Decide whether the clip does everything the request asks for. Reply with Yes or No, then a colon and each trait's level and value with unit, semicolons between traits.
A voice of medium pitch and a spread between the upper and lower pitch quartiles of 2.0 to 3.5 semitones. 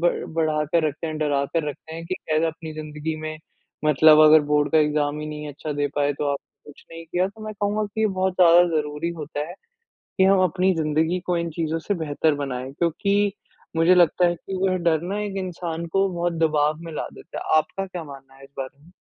Yes: medium, 160 Hz; average, 2.8 semitones